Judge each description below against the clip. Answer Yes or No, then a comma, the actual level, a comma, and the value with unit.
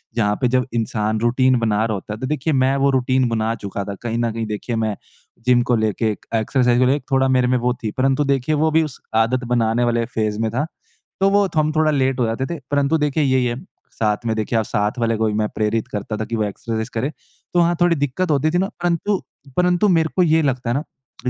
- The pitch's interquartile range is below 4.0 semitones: No, average, 4.3 semitones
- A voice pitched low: Yes, low, 125 Hz